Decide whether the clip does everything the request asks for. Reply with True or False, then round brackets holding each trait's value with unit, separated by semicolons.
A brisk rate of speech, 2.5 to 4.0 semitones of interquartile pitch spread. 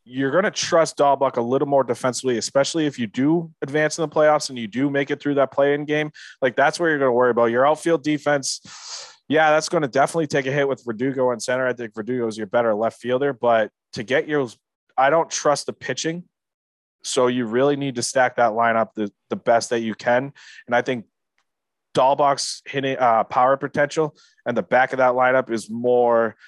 True (220 wpm; 3.5 semitones)